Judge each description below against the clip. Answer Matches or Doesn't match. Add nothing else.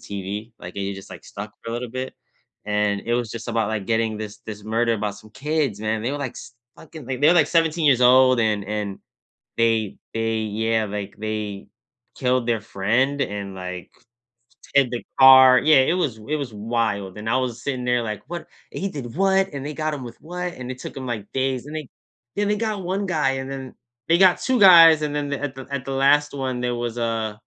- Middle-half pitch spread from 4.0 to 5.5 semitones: Matches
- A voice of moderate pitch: Doesn't match